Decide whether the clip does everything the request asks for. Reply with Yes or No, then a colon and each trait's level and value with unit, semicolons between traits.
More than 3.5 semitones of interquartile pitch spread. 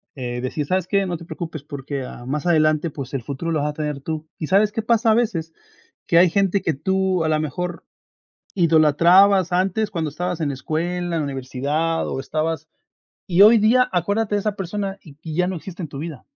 Yes: average, 4.1 semitones